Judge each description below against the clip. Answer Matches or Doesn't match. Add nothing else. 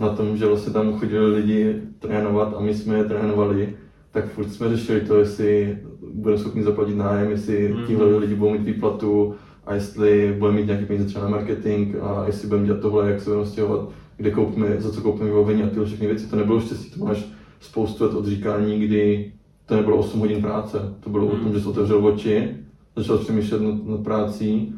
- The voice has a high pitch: Doesn't match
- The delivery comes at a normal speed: Doesn't match